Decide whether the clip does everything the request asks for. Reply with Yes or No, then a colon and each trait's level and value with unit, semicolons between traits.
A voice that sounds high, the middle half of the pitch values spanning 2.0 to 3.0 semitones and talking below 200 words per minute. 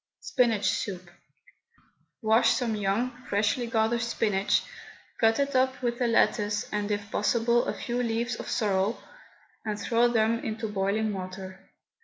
Yes: high, 220 Hz; narrow, 2.5 semitones; average, 140 wpm